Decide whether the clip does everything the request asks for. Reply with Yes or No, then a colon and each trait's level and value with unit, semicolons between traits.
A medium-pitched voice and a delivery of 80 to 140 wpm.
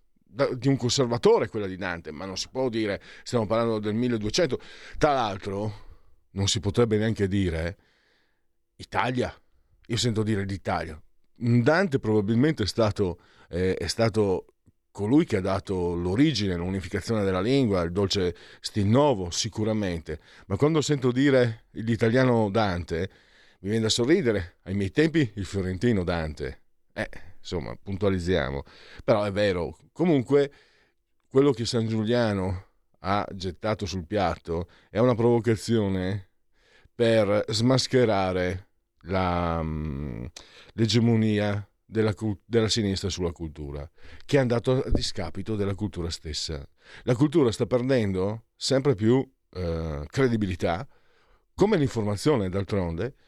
No: low, 105 Hz; average, 125 wpm